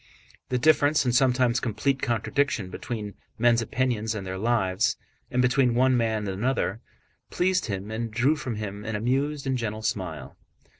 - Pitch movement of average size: Yes, average, 3.6 semitones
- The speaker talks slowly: No, average, 160 wpm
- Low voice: Yes, low, 120 Hz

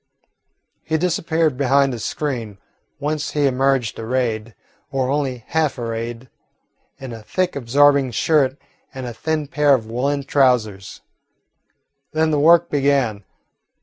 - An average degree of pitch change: Yes, average, 3.7 semitones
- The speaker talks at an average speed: No, slow, 125 wpm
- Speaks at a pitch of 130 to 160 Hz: Yes, low, 135 Hz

